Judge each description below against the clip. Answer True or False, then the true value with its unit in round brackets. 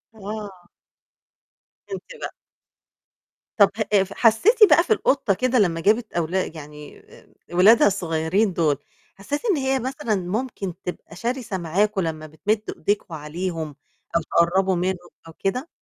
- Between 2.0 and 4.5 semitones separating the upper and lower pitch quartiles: False (4.9 semitones)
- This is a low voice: False (195 Hz)